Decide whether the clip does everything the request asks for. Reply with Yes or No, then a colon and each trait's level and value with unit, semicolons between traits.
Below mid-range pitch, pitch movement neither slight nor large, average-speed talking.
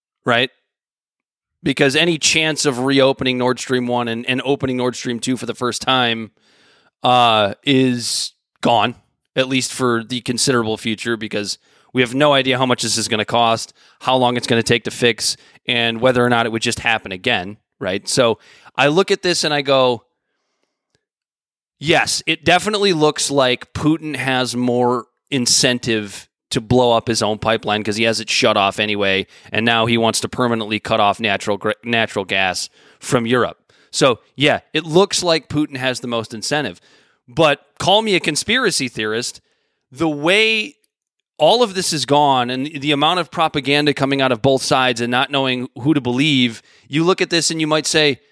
Yes: low, 125 Hz; average, 4.1 semitones; average, 180 wpm